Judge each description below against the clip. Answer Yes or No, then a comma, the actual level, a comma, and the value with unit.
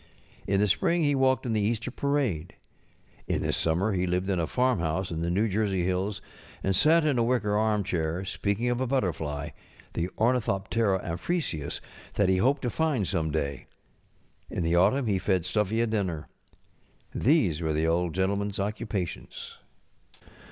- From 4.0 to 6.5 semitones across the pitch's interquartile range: Yes, average, 5.2 semitones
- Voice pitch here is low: Yes, low, 100 Hz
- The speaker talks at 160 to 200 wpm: Yes, average, 165 wpm